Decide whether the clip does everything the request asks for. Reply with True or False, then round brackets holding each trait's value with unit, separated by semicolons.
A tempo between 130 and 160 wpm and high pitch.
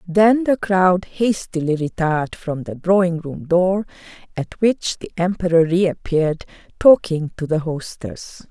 False (135 wpm; 175 Hz)